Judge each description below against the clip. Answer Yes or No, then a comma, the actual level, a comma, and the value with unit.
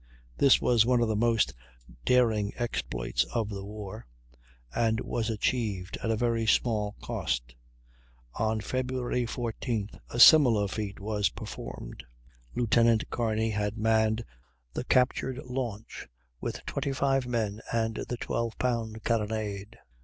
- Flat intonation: Yes, narrow, 2.2 semitones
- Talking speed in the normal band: No, slow, 125 wpm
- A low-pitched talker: Yes, low, 115 Hz